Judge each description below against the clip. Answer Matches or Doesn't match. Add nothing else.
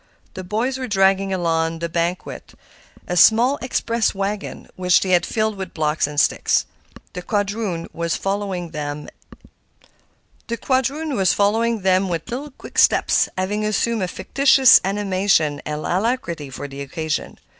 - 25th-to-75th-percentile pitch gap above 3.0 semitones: Matches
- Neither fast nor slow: Doesn't match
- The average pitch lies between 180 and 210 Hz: Matches